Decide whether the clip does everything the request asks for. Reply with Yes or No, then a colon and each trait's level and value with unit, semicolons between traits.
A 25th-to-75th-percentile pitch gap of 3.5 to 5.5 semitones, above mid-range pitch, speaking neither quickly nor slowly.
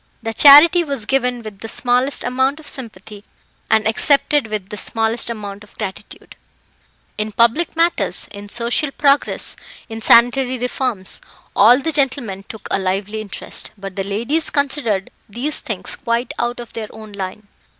Yes: average, 4.4 semitones; high, 235 Hz; average, 155 wpm